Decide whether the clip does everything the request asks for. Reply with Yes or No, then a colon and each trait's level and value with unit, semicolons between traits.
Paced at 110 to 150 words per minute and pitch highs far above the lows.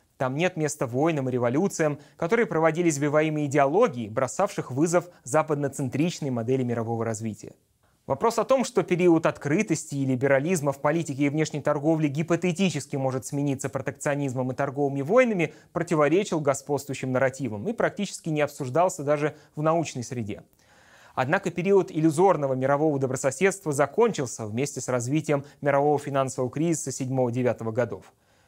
No: average, 130 wpm; average, 3.4 semitones